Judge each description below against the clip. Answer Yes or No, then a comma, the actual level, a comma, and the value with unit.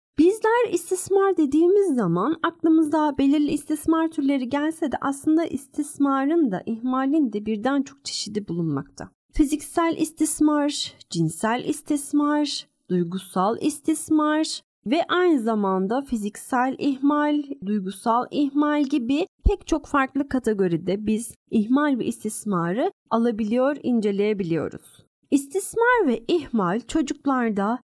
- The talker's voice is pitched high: Yes, very high, 285 Hz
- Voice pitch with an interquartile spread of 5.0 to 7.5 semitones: Yes, wide, 5.6 semitones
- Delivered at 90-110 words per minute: Yes, average, 100 wpm